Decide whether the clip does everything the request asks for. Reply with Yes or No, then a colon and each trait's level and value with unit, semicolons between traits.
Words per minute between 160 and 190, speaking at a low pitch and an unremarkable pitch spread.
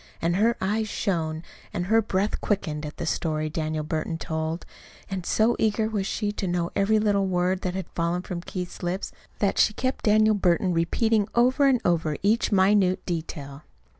No: average, 180 wpm; medium, 185 Hz; average, 4.1 semitones